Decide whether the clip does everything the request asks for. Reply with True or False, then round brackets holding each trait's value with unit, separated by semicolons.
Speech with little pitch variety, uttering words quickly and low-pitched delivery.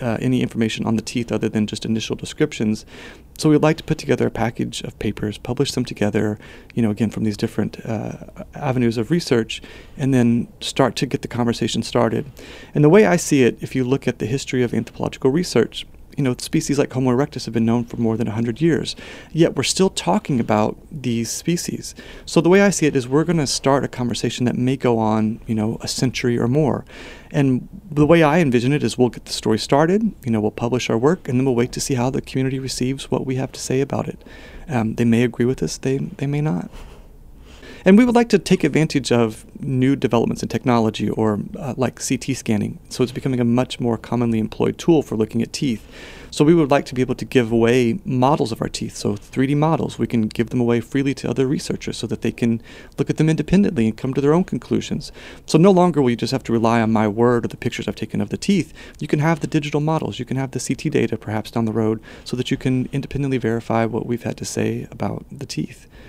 False (4.0 semitones; 240 wpm; 125 Hz)